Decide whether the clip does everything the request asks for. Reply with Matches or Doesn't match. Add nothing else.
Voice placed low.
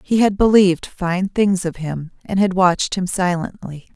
Doesn't match